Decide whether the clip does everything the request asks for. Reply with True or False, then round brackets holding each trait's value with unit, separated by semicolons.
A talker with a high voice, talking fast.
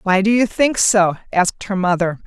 True (200 Hz; 210 wpm)